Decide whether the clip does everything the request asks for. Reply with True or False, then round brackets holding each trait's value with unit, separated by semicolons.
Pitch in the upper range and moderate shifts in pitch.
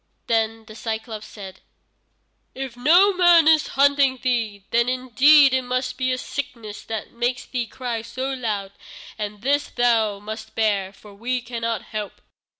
True (240 Hz; 3.2 semitones)